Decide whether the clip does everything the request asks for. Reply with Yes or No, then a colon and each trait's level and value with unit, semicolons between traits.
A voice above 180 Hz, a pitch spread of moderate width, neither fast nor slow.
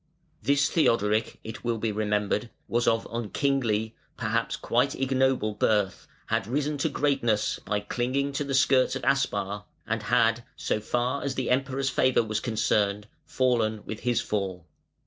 No: low, 120 Hz; average, 4.0 semitones; average, 155 wpm